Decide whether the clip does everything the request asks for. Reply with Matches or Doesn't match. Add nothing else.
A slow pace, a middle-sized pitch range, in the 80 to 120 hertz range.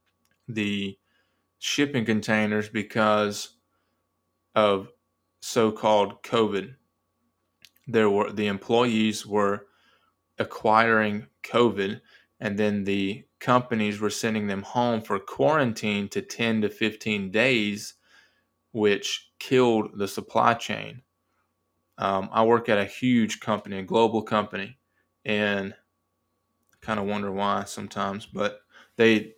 Doesn't match